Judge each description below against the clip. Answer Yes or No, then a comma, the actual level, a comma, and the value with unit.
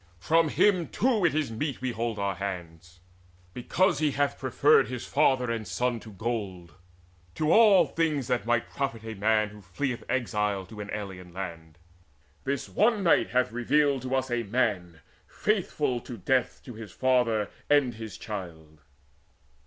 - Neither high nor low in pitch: No, low, 120 Hz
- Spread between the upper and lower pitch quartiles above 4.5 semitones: Yes, wide, 5.5 semitones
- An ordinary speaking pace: Yes, average, 160 wpm